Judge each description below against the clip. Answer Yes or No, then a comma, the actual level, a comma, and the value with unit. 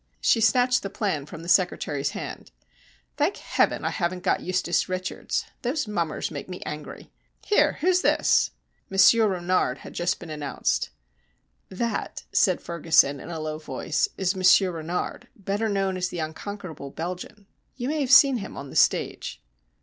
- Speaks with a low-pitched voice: No, medium, 185 Hz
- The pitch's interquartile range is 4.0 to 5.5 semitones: Yes, average, 4.5 semitones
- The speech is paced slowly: No, average, 160 wpm